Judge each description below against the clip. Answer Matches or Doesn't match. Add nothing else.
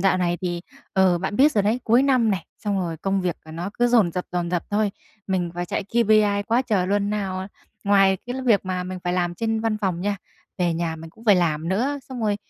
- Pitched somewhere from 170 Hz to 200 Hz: Matches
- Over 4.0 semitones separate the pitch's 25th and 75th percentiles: Doesn't match